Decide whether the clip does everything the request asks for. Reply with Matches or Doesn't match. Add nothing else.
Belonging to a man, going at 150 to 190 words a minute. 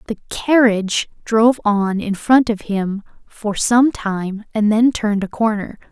Doesn't match